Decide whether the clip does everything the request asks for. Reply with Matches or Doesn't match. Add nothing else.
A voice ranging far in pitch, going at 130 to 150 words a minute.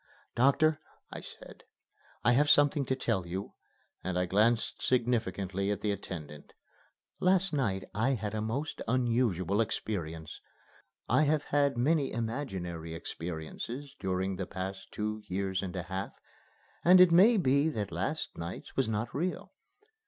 Matches